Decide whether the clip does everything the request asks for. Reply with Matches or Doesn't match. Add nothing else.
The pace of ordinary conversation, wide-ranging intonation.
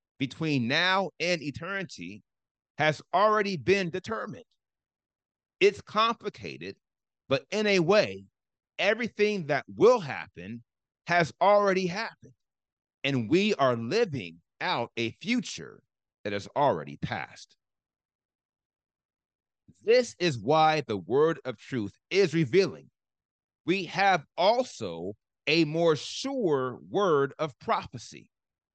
Doesn't match